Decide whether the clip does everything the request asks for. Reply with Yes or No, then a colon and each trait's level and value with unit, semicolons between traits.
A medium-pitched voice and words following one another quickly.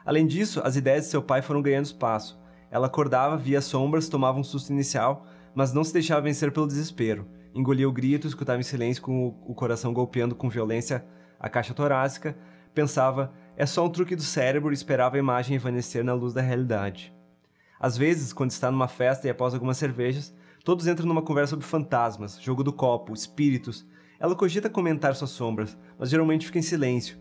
No: low, 130 Hz; fast, 190 wpm